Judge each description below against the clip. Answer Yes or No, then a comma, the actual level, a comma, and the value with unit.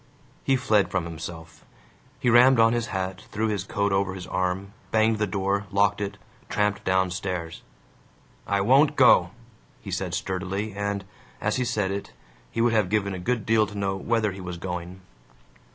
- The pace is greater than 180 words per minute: No, average, 175 wpm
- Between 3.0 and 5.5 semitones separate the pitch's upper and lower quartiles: No, narrow, 2.6 semitones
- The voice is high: No, low, 100 Hz